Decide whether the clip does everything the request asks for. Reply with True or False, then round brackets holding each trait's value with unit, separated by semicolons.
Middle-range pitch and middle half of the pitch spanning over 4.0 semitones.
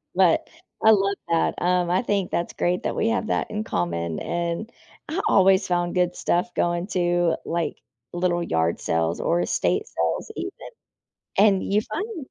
False (180 Hz; 2.8 semitones)